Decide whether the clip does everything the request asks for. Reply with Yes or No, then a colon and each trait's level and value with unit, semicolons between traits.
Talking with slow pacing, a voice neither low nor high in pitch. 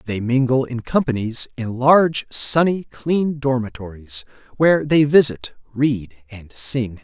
No: slow, 130 wpm; low, 125 Hz